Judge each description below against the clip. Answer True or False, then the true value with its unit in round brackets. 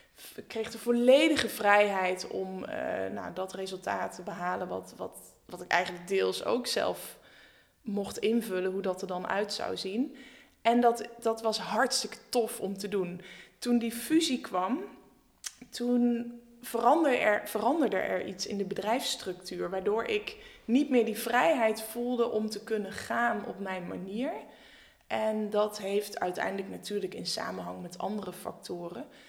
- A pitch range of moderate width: True (3.9 semitones)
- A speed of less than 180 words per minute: True (155 wpm)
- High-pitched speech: True (220 Hz)